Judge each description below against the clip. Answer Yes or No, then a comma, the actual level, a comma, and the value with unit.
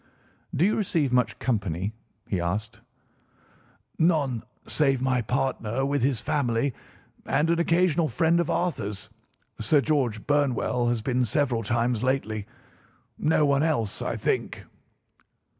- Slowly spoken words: Yes, slow, 125 wpm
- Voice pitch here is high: No, low, 130 Hz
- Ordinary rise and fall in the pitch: Yes, average, 4.8 semitones